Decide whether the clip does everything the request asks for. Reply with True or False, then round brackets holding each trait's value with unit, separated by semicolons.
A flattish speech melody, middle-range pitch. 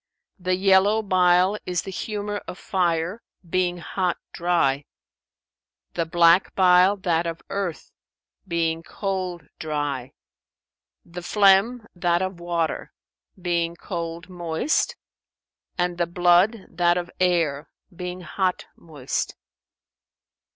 True (2.0 semitones; 175 Hz)